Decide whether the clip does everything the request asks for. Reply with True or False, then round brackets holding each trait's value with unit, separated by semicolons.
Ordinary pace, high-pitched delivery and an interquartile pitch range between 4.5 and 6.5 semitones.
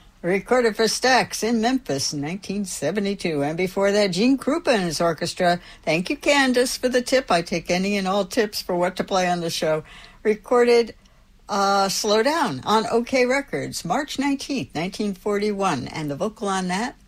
True (185 wpm; 205 Hz; 5.1 semitones)